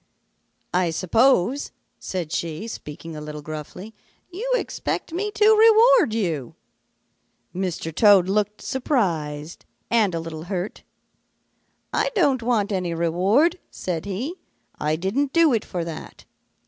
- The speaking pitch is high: Yes, high, 195 Hz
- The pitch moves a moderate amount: No, wide, 8.2 semitones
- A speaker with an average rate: No, slow, 125 wpm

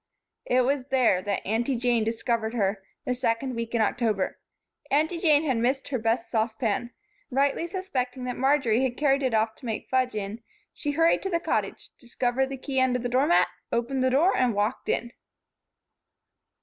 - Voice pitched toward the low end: No, very high, 250 Hz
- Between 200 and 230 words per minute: No, average, 180 wpm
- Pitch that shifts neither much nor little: Yes, average, 3.1 semitones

